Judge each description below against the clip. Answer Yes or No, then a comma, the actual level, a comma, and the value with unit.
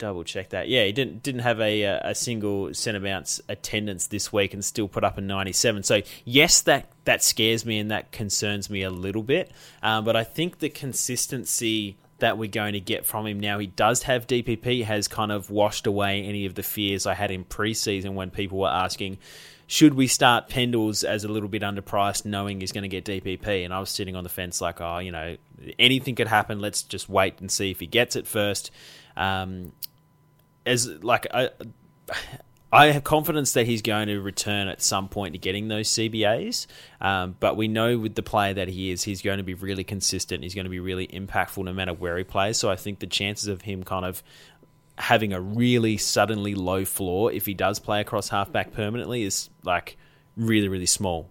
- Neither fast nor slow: No, fast, 210 wpm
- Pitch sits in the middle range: No, low, 105 Hz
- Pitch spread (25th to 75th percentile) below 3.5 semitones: Yes, average, 2.9 semitones